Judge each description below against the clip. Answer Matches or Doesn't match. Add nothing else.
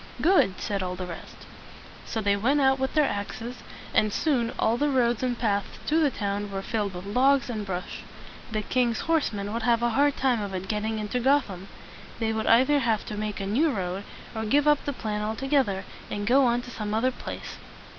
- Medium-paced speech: Doesn't match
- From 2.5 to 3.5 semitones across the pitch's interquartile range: Doesn't match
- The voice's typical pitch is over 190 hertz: Matches